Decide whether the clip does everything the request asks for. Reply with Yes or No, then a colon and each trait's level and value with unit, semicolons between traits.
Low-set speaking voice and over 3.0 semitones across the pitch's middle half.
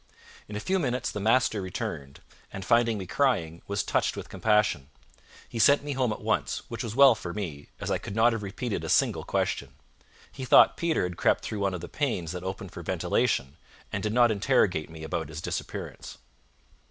Yes: low, 105 Hz; average, 5.2 semitones